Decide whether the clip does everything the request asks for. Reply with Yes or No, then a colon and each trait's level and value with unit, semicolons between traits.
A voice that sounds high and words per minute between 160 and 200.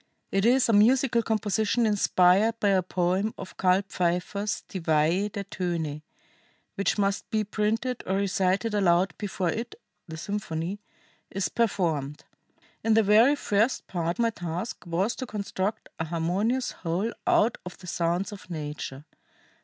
No: high, 195 Hz; average, 145 wpm